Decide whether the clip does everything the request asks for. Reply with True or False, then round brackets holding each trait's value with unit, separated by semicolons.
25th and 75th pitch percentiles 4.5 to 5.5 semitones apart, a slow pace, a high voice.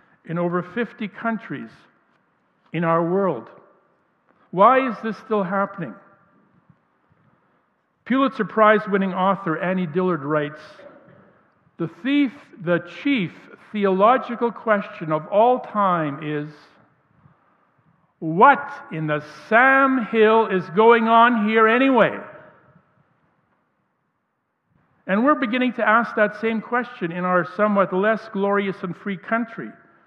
True (4.8 semitones; 110 wpm; 200 Hz)